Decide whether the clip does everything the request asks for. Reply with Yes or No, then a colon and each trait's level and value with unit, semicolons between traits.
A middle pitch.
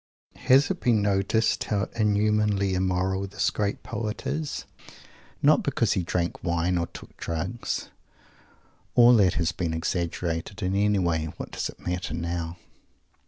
No: very low, 95 Hz